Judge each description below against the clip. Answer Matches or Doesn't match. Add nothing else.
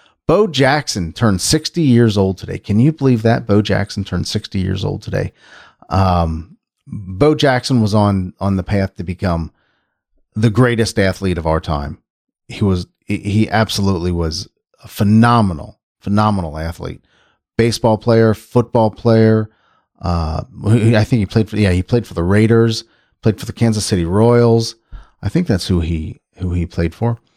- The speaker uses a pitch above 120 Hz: Doesn't match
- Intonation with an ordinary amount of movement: Matches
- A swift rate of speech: Doesn't match